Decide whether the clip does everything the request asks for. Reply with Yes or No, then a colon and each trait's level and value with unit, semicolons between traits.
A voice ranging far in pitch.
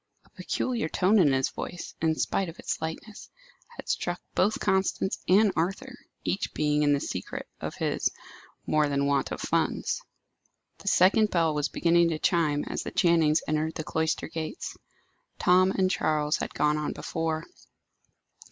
No: average, 3.6 semitones